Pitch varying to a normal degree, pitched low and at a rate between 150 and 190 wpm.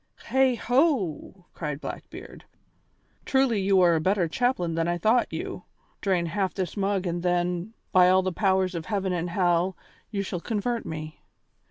No: average, 3.1 semitones; medium, 185 Hz; average, 160 wpm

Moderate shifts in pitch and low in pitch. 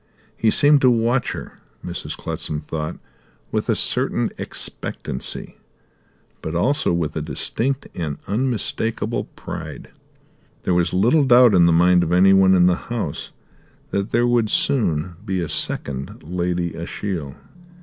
No: wide, 5.9 semitones; very low, 90 Hz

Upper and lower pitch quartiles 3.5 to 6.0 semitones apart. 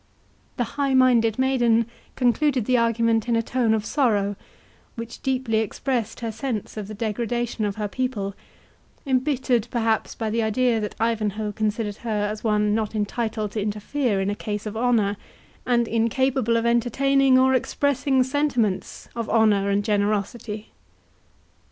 No: average, 3.0 semitones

